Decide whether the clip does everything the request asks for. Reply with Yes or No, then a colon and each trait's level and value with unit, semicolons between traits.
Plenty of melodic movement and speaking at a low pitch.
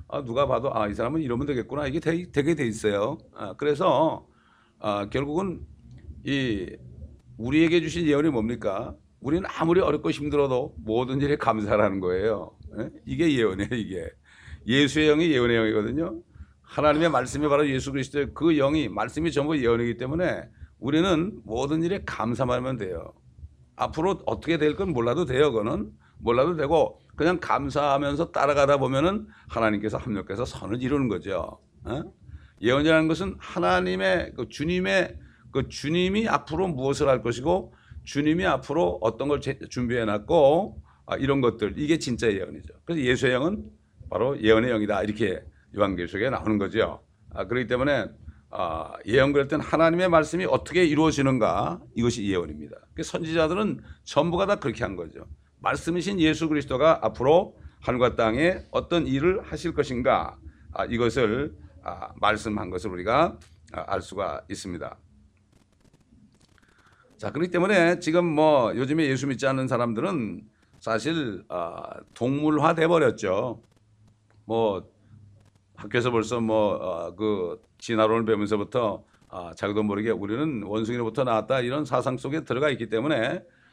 Yes: wide, 6.2 semitones; low, 130 Hz